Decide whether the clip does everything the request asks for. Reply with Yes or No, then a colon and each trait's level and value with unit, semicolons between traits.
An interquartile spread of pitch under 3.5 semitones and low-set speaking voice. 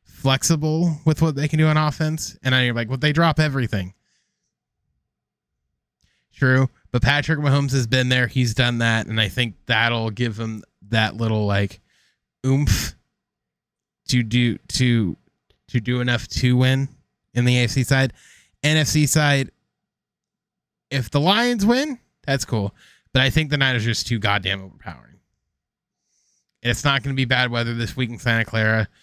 No: average, 3.8 semitones; low, 125 Hz